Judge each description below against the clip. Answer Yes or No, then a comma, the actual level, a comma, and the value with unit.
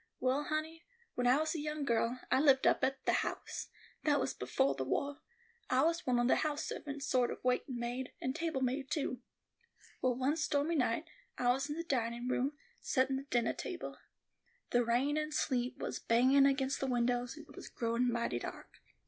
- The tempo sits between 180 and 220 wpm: Yes, average, 200 wpm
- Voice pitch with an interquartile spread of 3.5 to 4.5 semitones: No, average, 3.1 semitones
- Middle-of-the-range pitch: No, very high, 260 Hz